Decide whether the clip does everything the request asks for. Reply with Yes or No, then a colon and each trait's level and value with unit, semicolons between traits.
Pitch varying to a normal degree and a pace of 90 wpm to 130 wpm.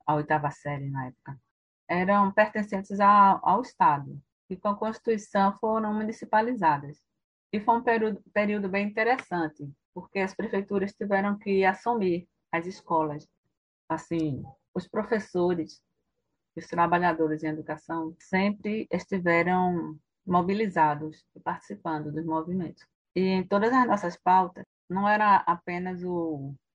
Yes: average, 4.4 semitones; slow, 120 wpm